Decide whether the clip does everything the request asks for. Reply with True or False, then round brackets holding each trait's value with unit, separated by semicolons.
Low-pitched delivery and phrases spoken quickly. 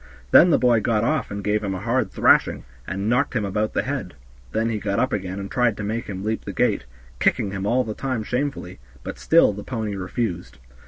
True (110 Hz; 225 wpm)